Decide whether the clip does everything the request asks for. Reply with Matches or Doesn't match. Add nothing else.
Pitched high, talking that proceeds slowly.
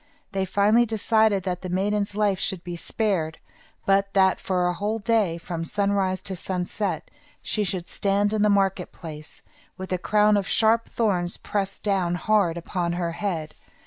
Doesn't match